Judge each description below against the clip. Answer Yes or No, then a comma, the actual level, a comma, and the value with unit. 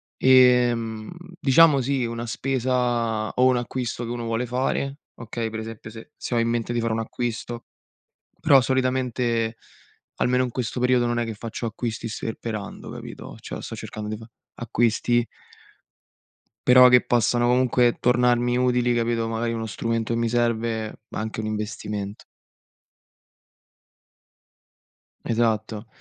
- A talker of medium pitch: No, low, 120 Hz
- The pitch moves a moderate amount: No, narrow, 1.7 semitones